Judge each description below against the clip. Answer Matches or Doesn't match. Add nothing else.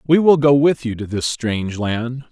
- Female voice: Doesn't match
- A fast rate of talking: Matches